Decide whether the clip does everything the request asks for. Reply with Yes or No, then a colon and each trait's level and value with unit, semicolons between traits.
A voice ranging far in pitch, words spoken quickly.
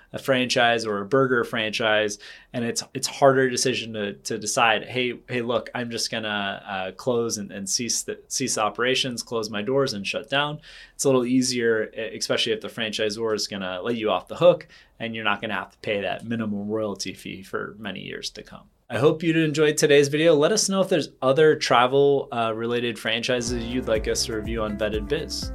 No: average, 3.7 semitones; fast, 210 wpm